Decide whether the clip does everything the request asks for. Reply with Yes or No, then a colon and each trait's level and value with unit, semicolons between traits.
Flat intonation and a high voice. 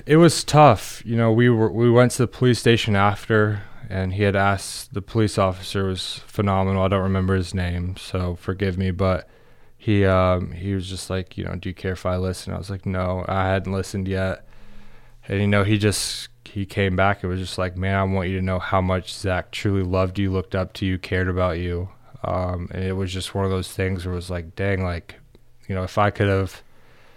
No: narrow, 2.0 semitones; very low, 95 Hz